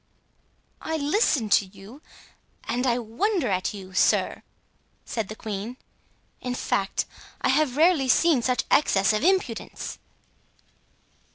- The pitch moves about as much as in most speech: No, wide, 6.1 semitones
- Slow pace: Yes, slow, 120 wpm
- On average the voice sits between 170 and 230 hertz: No, high, 245 Hz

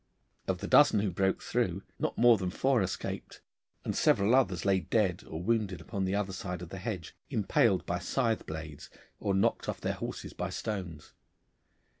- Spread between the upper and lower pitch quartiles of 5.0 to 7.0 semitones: No, average, 3.3 semitones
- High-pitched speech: No, very low, 95 Hz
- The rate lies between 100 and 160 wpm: No, average, 180 wpm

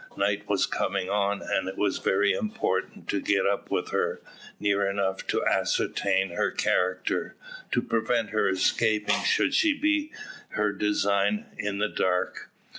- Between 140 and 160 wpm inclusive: Yes, average, 150 wpm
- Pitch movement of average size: No, narrow, 1.6 semitones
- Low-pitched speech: Yes, low, 100 Hz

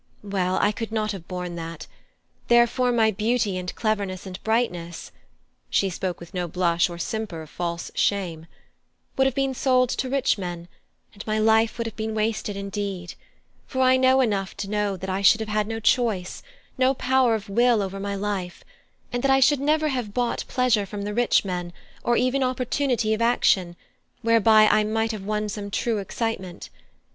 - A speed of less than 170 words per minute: No, average, 190 wpm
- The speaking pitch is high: Yes, high, 215 Hz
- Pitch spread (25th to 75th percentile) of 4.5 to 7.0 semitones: No, average, 3.9 semitones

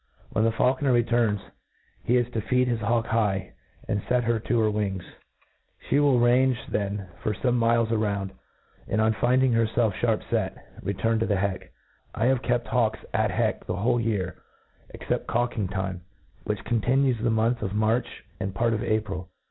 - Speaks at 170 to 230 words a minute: Yes, average, 185 wpm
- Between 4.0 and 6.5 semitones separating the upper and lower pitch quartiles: No, average, 2.8 semitones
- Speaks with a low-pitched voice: Yes, low, 115 Hz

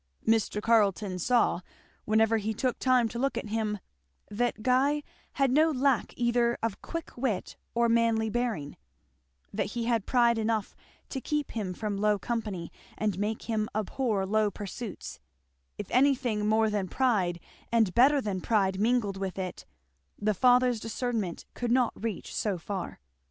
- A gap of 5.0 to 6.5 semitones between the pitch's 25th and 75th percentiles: No, average, 3.0 semitones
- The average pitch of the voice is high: Yes, high, 225 Hz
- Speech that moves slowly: No, average, 155 wpm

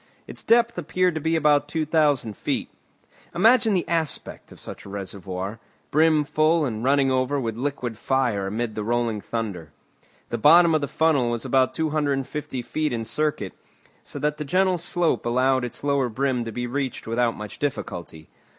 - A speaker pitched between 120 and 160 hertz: Yes, low, 135 Hz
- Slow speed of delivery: No, average, 175 wpm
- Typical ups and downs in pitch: Yes, average, 4.9 semitones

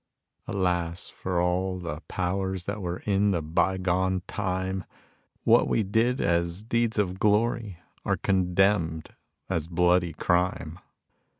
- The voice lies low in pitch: Yes, very low, 95 Hz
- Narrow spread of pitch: Yes, narrow, 2.1 semitones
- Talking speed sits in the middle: No, slow, 125 wpm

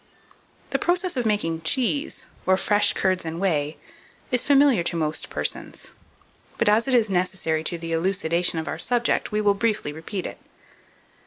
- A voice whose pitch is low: No, high, 190 Hz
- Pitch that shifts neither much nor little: No, wide, 5.8 semitones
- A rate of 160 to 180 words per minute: Yes, average, 165 wpm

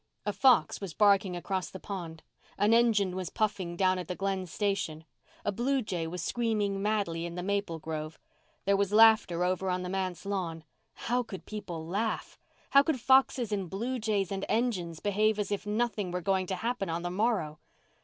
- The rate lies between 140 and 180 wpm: No, average, 190 wpm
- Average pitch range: Yes, average, 3.2 semitones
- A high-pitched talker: Yes, high, 195 Hz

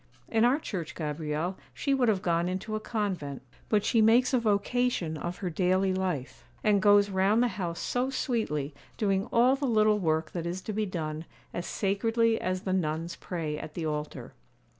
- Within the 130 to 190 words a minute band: Yes, average, 185 wpm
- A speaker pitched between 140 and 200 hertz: Yes, high, 190 Hz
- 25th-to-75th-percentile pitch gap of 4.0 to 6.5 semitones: Yes, average, 4.7 semitones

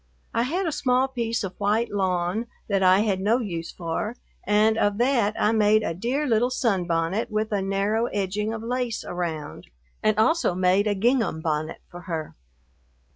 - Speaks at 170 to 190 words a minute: Yes, average, 175 wpm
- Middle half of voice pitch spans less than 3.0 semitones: No, average, 4.0 semitones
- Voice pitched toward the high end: Yes, high, 210 Hz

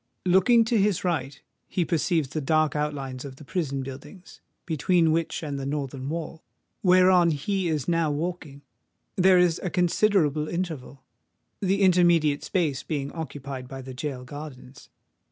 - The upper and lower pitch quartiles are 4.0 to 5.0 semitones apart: Yes, average, 4.3 semitones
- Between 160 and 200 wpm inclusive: No, average, 150 wpm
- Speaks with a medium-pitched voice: Yes, medium, 155 Hz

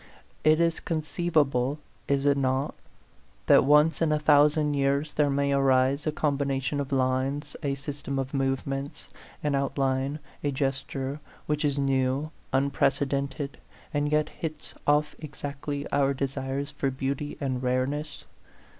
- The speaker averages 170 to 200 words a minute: No, slow, 135 wpm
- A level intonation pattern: Yes, narrow, 1.5 semitones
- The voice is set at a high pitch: No, medium, 140 Hz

